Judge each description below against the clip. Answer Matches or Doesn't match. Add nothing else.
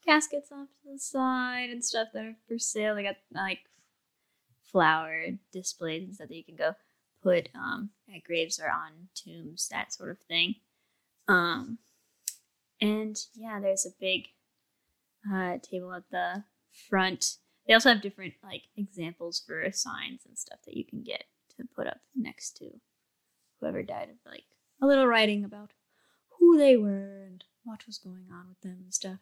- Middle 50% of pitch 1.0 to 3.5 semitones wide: Doesn't match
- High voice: Matches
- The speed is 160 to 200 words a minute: Matches